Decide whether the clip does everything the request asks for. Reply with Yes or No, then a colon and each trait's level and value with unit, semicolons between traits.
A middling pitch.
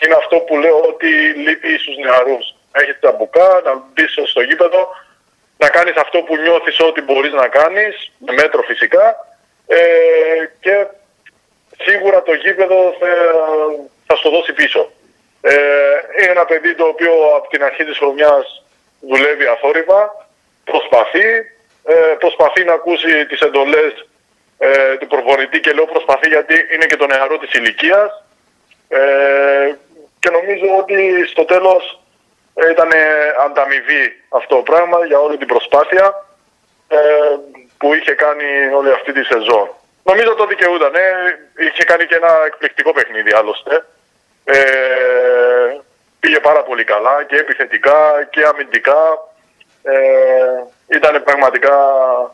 Yes: medium, 170 Hz